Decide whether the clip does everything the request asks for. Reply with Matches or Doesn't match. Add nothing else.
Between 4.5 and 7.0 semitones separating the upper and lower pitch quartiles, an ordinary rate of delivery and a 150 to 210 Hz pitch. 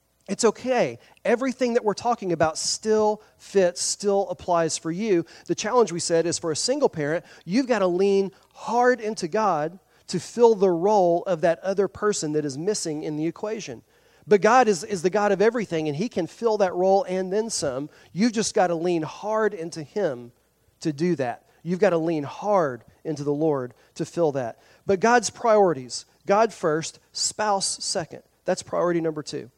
Matches